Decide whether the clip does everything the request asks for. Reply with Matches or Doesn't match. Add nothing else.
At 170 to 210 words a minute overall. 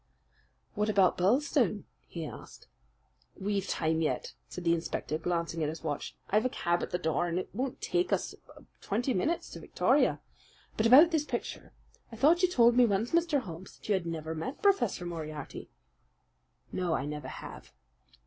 Matches